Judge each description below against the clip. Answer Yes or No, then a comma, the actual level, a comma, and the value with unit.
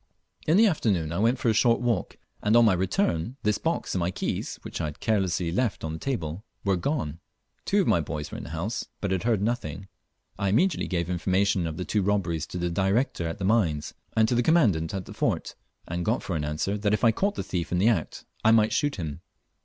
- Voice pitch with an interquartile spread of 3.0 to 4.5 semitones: No, average, 5.1 semitones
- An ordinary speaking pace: No, fast, 240 wpm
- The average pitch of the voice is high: No, low, 100 Hz